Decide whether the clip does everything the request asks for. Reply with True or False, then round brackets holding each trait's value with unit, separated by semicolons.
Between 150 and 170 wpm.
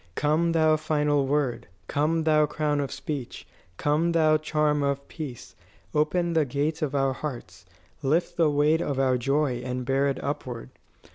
True (160 wpm)